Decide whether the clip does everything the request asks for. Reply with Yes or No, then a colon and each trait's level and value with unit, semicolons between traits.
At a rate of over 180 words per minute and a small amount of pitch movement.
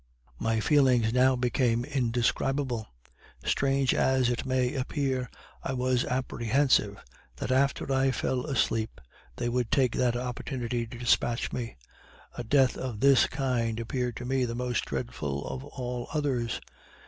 No: average, 140 wpm; narrow, 2.0 semitones